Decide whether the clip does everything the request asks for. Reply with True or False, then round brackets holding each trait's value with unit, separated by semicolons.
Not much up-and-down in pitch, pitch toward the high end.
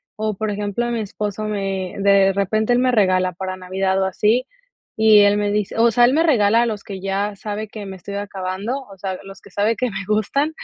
True (2.0 semitones; 205 Hz)